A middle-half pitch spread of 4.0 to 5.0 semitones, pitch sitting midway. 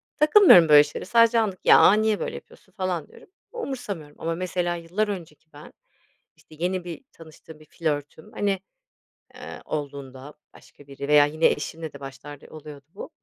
Yes: average, 4.4 semitones; medium, 165 Hz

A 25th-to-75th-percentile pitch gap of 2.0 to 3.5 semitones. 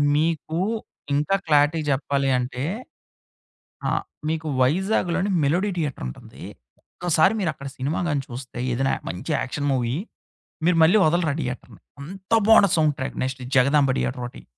No: average, 4.2 semitones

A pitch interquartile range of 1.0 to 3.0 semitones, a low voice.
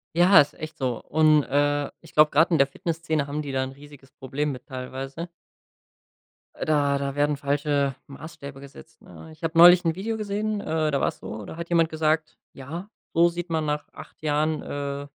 No: narrow, 2.6 semitones; medium, 150 Hz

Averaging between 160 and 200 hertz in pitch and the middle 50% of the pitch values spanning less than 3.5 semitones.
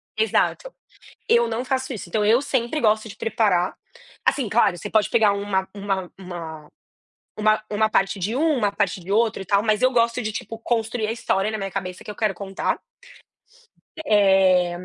No: high, 215 Hz; average, 3.1 semitones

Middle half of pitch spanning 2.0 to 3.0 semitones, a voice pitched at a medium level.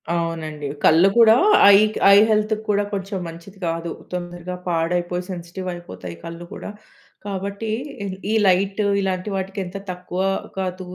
Yes: narrow, 2.6 semitones; medium, 180 Hz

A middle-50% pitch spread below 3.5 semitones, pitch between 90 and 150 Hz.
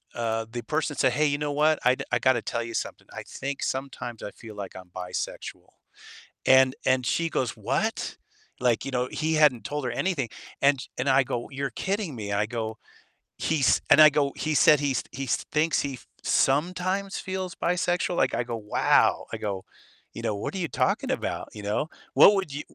No: average, 4.6 semitones; low, 135 Hz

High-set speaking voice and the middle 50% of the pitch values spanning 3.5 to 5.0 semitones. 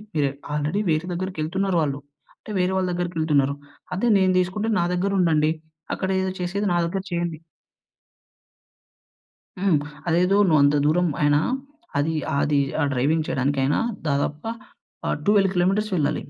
No: medium, 175 Hz; average, 4.1 semitones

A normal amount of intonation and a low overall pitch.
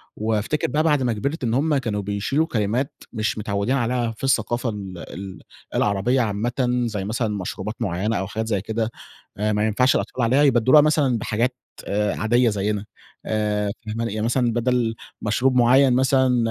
Yes: average, 3.3 semitones; low, 115 Hz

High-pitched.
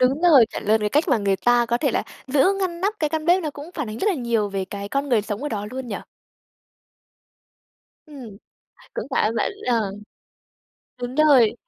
Yes: very high, 250 Hz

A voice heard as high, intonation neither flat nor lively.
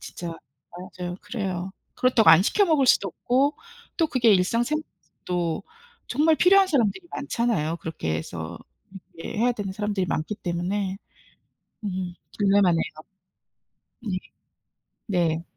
No: high, 200 Hz; wide, 5.9 semitones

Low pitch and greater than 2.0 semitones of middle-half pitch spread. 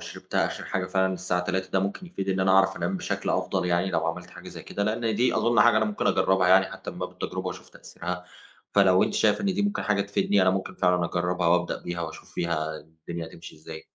Yes: very low, 95 Hz; narrow, 2.4 semitones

